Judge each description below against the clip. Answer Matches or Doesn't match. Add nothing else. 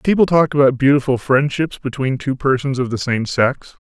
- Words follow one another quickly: Doesn't match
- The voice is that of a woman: Doesn't match